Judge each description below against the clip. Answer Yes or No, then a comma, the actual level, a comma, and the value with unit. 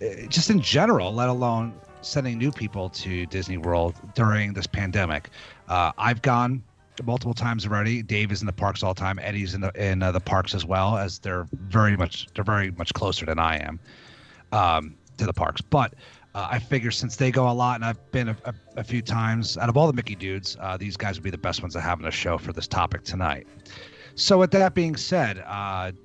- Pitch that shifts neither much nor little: Yes, average, 4.2 semitones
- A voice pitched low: Yes, low, 105 Hz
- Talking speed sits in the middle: No, fast, 225 wpm